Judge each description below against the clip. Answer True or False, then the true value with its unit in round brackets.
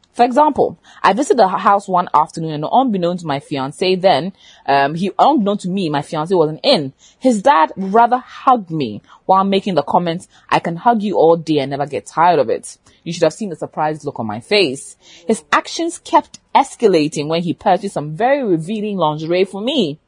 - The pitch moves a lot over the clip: True (5.9 semitones)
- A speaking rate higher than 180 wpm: True (200 wpm)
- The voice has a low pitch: False (180 Hz)